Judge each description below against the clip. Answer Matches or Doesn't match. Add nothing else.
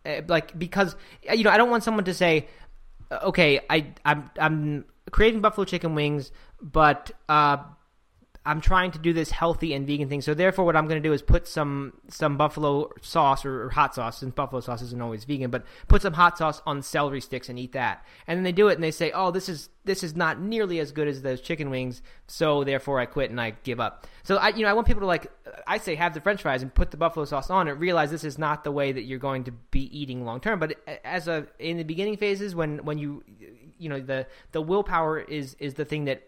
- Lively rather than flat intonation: Doesn't match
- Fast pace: Matches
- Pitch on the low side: Doesn't match